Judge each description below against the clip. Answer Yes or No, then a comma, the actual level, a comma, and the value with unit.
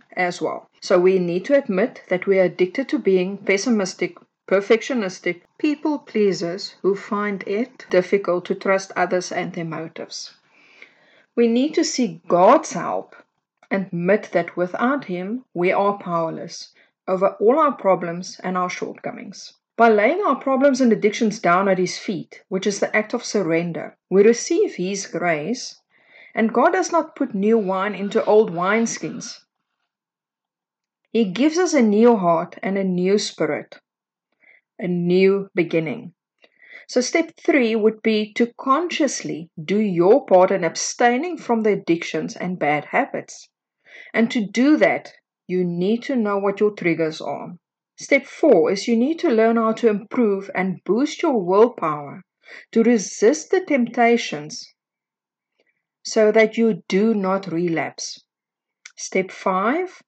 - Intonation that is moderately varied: Yes, average, 4.6 semitones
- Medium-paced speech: Yes, average, 150 wpm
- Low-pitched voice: No, high, 210 Hz